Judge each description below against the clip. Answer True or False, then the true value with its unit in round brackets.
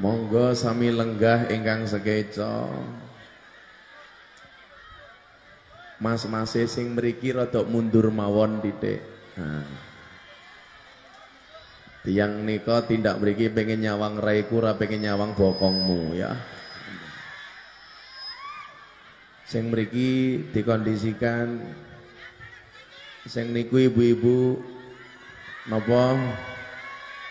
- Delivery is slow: True (70 wpm)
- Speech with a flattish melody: True (2.1 semitones)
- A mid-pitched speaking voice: False (115 Hz)